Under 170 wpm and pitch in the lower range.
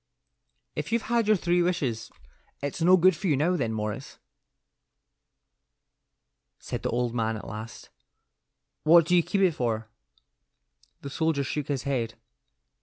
No: average, 145 wpm; medium, 145 Hz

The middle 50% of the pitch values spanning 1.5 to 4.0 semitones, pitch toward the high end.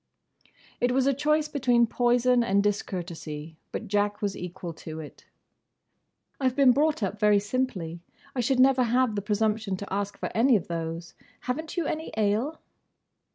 No: average, 5.0 semitones; high, 220 Hz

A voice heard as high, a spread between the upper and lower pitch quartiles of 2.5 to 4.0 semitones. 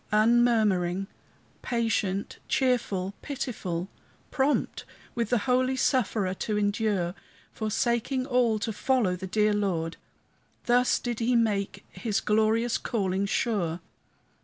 Yes: high, 215 Hz; average, 3.5 semitones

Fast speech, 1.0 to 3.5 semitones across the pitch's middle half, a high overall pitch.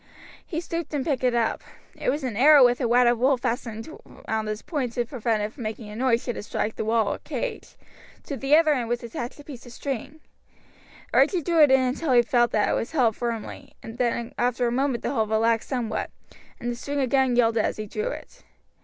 Yes: fast, 230 wpm; average, 3.2 semitones; high, 245 Hz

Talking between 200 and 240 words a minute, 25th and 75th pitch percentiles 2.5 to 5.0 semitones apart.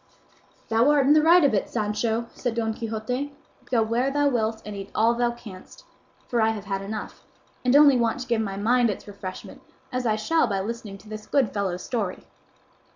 Yes: fast, 205 wpm; average, 3.0 semitones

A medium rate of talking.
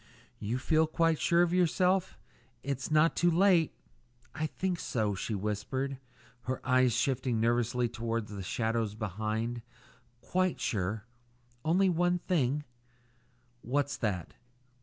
No: slow, 130 wpm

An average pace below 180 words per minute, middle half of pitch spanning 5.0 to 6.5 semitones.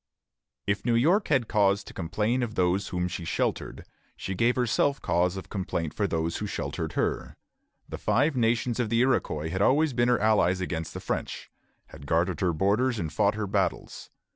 No: average, 190 wpm; average, 5.3 semitones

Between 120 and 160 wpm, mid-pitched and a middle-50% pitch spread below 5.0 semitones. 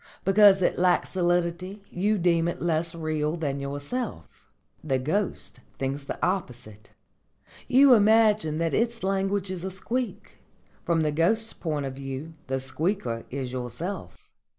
No: average, 140 wpm; medium, 170 Hz; wide, 5.6 semitones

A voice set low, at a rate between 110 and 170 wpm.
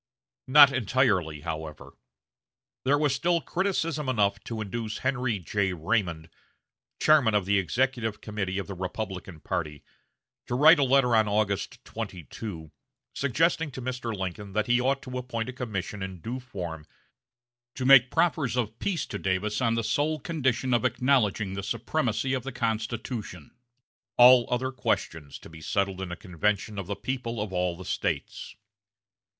Yes: low, 115 Hz; average, 155 wpm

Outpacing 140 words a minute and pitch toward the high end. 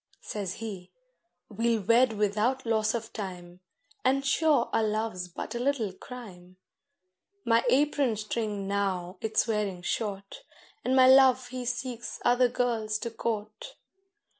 No: slow, 135 wpm; high, 225 Hz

